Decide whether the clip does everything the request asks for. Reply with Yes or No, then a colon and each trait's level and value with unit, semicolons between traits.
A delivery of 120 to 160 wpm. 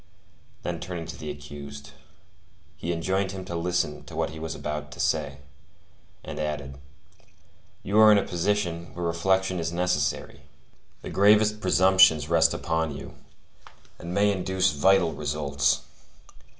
Yes: average, 140 wpm